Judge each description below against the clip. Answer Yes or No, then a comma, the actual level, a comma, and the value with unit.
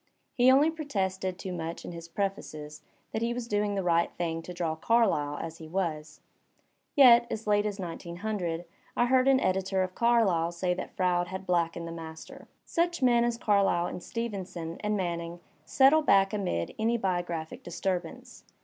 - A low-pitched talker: No, high, 190 Hz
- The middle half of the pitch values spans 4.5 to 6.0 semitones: Yes, average, 4.9 semitones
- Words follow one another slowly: No, average, 170 wpm